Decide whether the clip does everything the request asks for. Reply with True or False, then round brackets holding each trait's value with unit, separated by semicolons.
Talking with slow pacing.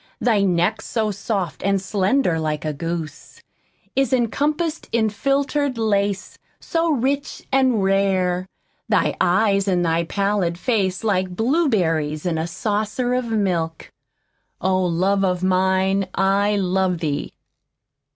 True (125 wpm)